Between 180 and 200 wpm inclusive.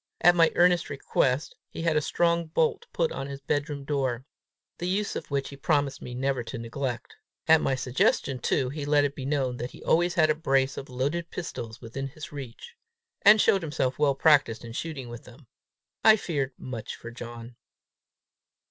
Yes: average, 190 wpm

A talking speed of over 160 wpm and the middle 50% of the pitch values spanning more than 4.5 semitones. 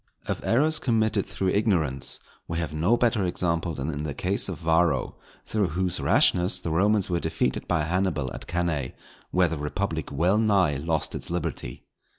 No: average, 170 wpm; average, 3.8 semitones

